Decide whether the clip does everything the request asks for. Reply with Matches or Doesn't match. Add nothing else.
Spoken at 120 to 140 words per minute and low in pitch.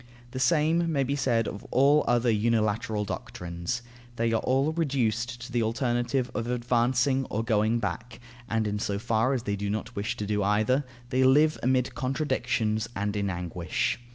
Doesn't match